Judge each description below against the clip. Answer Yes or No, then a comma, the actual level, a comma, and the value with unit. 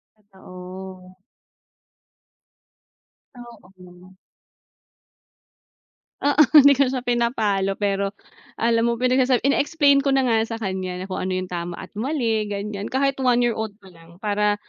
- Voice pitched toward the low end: No, high, 210 Hz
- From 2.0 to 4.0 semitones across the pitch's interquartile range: No, average, 4.8 semitones